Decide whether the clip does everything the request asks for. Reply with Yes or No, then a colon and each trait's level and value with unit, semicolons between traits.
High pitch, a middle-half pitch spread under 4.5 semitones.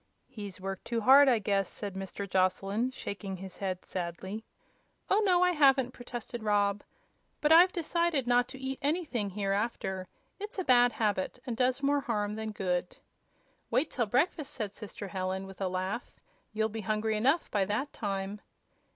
No: high, 220 Hz; average, 5.3 semitones